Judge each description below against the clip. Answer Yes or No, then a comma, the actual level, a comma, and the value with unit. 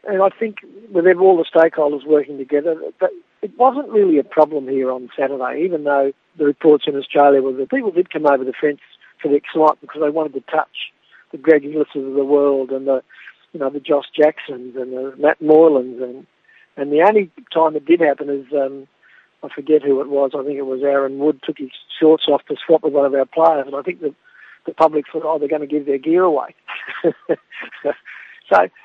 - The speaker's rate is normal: No, fast, 220 wpm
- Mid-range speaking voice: Yes, medium, 150 Hz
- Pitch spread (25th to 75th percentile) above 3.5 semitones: No, average, 2.8 semitones